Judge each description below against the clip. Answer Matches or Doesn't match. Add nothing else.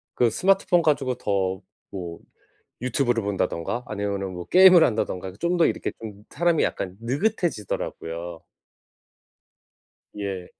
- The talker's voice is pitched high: Doesn't match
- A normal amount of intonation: Doesn't match